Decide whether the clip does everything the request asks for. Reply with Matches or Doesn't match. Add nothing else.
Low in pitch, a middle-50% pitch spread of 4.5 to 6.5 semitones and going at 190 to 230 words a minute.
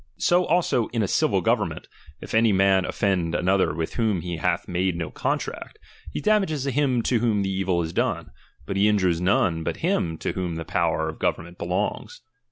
Matches